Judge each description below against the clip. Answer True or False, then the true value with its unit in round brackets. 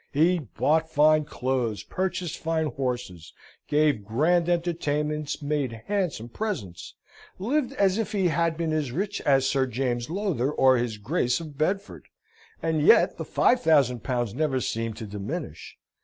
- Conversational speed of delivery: True (150 wpm)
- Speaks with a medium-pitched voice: True (150 Hz)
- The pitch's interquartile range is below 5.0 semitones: False (5.4 semitones)